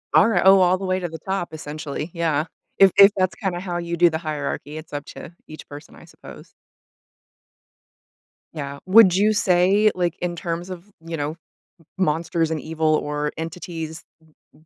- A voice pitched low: No, medium, 170 Hz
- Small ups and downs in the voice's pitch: No, average, 3.0 semitones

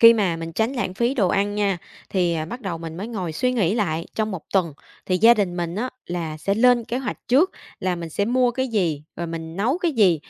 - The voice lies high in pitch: Yes, high, 195 Hz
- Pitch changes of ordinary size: No, wide, 5.7 semitones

